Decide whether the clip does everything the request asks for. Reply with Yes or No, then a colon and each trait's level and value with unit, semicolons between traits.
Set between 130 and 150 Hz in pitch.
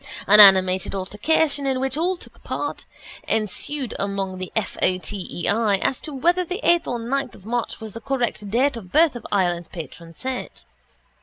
No: high, 225 Hz